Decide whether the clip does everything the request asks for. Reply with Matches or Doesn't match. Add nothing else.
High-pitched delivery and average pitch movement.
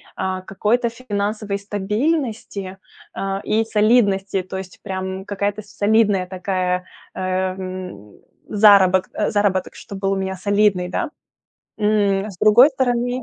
Doesn't match